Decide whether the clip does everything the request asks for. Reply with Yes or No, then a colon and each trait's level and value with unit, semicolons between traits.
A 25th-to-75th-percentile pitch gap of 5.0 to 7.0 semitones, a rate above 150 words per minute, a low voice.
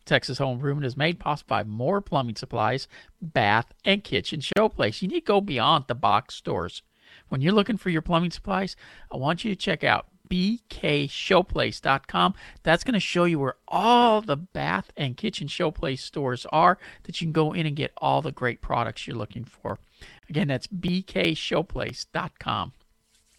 No: wide, 5.5 semitones; average, 170 wpm; medium, 160 Hz